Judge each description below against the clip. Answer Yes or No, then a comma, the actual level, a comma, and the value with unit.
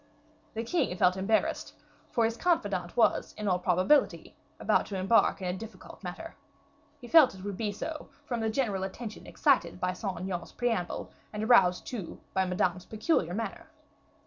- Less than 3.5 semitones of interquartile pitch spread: No, average, 4.2 semitones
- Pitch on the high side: Yes, high, 205 Hz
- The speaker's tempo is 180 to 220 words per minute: No, average, 170 wpm